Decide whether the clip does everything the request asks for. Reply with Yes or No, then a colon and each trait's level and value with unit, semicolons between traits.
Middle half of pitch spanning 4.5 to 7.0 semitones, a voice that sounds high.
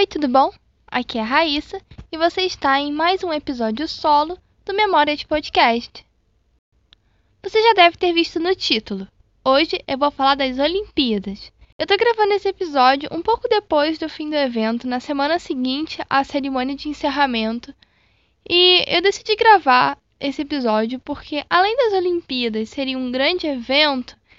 Yes: average, 4.8 semitones; very high, 295 Hz